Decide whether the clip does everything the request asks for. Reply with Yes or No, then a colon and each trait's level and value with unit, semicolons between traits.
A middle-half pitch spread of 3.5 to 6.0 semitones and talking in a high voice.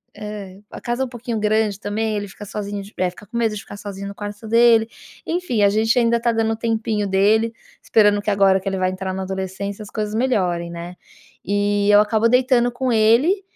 No: narrow, 2.4 semitones; high, 210 Hz